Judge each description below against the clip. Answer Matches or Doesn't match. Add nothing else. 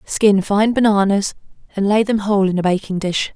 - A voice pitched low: Doesn't match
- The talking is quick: Doesn't match